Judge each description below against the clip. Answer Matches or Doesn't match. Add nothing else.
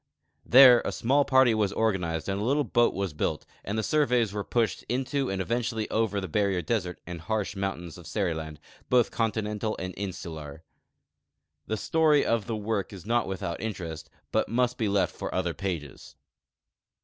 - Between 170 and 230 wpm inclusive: Matches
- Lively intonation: Doesn't match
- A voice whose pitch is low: Matches